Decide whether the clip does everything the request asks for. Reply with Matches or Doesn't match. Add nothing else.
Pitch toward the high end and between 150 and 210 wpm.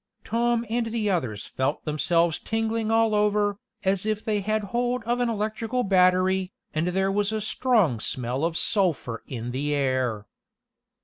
Matches